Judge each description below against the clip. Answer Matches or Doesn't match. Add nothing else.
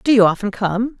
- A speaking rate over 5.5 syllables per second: Doesn't match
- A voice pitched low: Doesn't match